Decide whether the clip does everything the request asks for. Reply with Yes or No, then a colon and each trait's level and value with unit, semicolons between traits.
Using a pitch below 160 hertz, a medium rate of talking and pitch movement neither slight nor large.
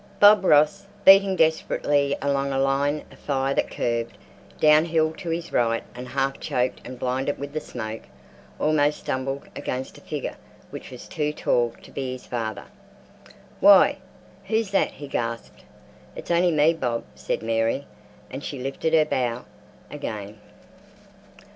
Yes: medium, 140 Hz; average, 150 wpm; average, 4.0 semitones